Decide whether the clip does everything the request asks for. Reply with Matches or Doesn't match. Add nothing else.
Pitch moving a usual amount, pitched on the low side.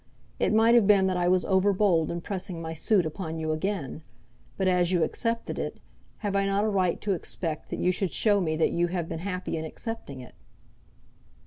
Doesn't match